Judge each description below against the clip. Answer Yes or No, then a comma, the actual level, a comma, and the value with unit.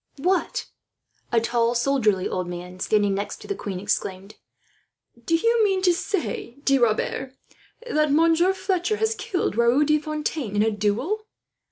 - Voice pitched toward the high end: Yes, very high, 275 Hz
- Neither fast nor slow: Yes, average, 155 wpm